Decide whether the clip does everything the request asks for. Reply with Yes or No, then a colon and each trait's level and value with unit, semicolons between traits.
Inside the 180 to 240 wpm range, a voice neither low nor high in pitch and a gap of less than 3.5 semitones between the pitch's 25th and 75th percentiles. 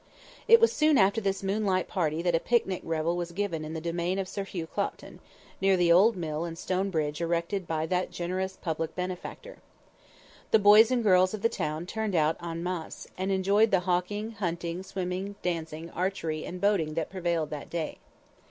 Yes: average, 190 wpm; medium, 180 Hz; average, 2.9 semitones